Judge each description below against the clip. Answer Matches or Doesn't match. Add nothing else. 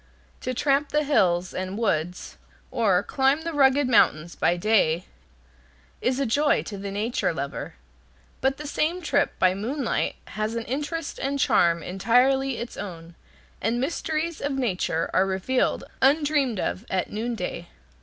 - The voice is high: Matches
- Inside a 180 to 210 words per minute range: Doesn't match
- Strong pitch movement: Matches